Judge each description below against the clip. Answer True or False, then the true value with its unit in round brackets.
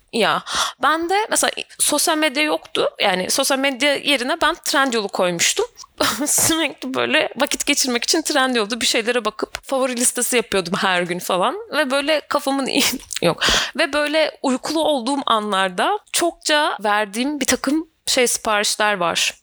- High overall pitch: True (275 Hz)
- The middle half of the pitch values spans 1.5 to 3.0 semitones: False (4.3 semitones)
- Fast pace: True (145 wpm)